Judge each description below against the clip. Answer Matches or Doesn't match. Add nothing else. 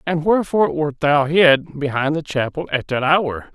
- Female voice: Doesn't match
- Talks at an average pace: Matches